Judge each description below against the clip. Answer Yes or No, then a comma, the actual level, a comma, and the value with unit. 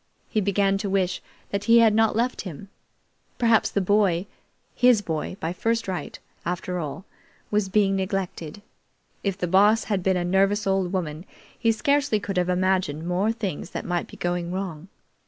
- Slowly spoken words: No, average, 175 wpm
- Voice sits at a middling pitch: No, high, 195 Hz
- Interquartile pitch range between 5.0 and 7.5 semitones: No, average, 2.8 semitones